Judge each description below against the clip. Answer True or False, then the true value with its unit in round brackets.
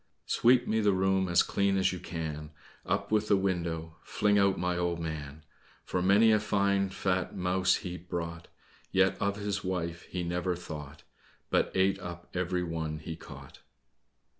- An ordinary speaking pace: True (165 wpm)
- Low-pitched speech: True (90 Hz)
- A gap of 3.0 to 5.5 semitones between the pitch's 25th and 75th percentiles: False (2.6 semitones)